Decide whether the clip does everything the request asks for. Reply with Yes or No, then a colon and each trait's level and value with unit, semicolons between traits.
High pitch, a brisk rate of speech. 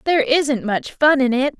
Yes: very high, 265 Hz; fast, 225 wpm